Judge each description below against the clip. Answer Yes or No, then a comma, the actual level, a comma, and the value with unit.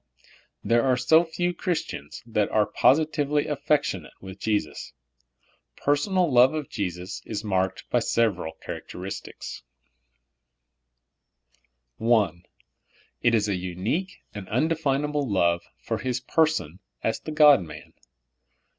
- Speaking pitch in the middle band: No, low, 120 Hz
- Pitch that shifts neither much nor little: No, wide, 7.7 semitones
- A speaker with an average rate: No, slow, 115 wpm